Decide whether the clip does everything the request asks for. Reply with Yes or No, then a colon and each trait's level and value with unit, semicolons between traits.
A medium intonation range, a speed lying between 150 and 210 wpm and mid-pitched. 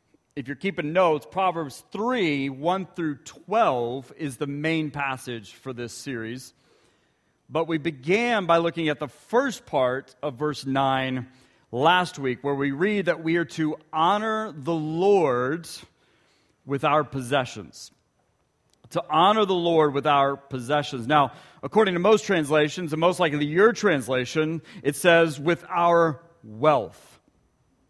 No: average, 4.0 semitones; average, 140 wpm; medium, 155 Hz